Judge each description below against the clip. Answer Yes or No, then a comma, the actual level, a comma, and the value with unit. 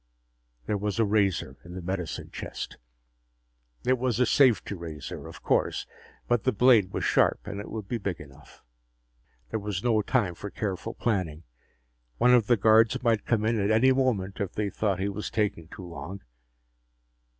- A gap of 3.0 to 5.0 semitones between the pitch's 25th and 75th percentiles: Yes, average, 3.5 semitones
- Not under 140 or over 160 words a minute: No, average, 175 wpm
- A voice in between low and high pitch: No, low, 105 Hz